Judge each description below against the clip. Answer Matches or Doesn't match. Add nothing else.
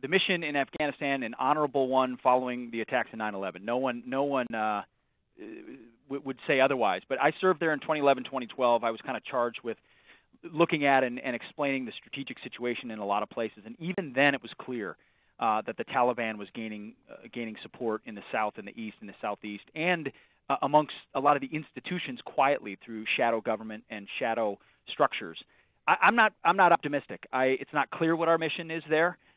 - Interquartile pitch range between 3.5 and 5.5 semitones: Matches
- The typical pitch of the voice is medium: Doesn't match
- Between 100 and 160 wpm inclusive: Doesn't match